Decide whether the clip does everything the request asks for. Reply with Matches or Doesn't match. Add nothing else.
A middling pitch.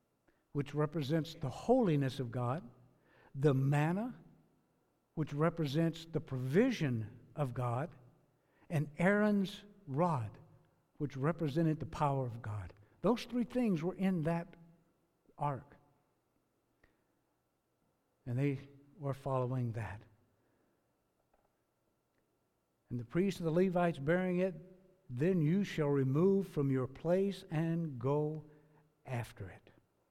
Matches